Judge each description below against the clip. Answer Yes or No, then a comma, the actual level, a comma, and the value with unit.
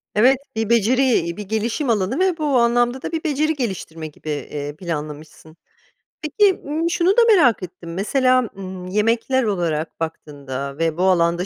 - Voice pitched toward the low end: No, high, 210 Hz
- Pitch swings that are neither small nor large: No, wide, 8.0 semitones